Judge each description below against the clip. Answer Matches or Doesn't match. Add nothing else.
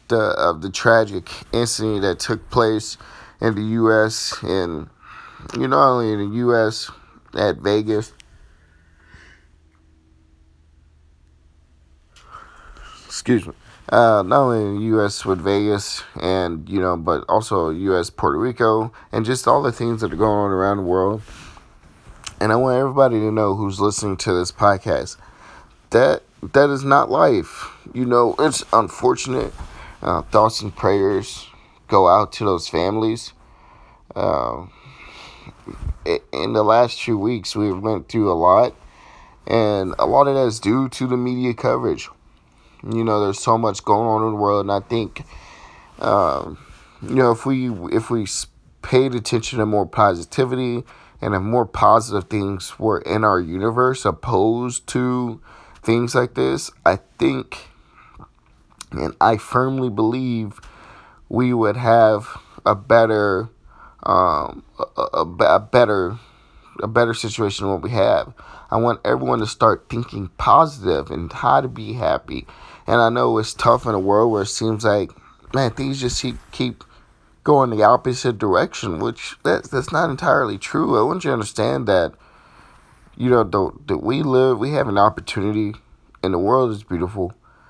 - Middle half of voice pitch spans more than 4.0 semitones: Doesn't match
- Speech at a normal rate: Matches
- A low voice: Matches